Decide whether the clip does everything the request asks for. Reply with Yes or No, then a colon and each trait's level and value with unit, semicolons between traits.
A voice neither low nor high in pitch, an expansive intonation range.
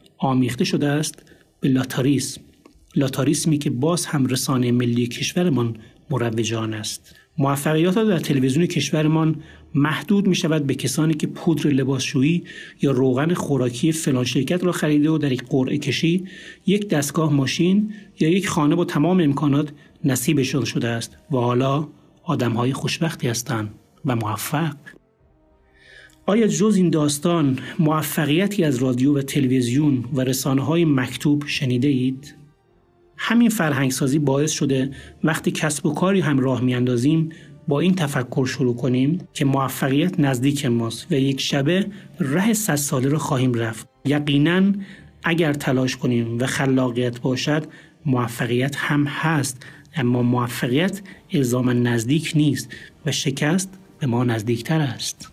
No: medium, 145 Hz; average, 3.7 semitones